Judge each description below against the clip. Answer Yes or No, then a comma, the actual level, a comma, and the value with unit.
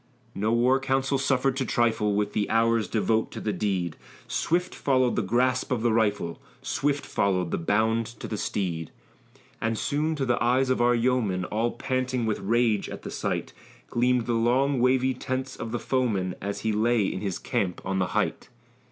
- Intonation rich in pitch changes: No, average, 3.6 semitones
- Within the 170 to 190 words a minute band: Yes, average, 185 wpm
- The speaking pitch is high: No, low, 115 Hz